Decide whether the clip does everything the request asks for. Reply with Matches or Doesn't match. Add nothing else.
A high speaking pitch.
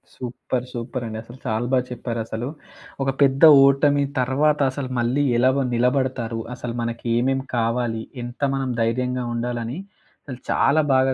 Doesn't match